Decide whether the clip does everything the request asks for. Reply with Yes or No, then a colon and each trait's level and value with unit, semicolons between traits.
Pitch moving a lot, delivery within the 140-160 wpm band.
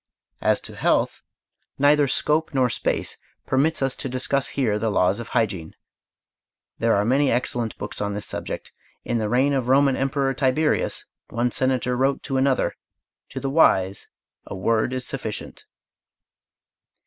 No: average, 3.5 semitones; average, 155 wpm